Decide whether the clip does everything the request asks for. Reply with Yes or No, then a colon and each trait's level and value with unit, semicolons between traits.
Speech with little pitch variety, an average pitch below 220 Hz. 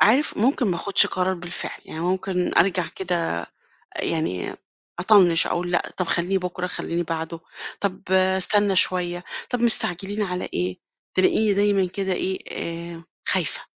Yes: narrow, 2.1 semitones; medium, 185 Hz